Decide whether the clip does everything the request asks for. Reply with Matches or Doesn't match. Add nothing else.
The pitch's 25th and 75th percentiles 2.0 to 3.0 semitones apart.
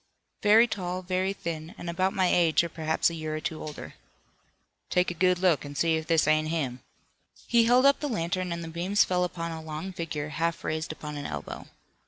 Matches